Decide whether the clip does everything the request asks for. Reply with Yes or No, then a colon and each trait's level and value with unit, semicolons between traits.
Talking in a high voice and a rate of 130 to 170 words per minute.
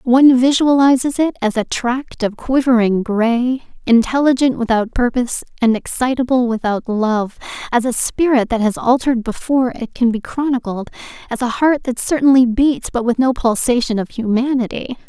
Yes: high, 245 Hz; average, 155 wpm